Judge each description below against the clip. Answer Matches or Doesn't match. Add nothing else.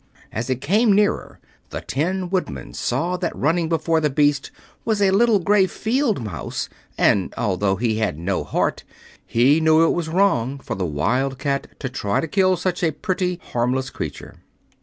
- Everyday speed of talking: Matches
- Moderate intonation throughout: Doesn't match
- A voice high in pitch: Doesn't match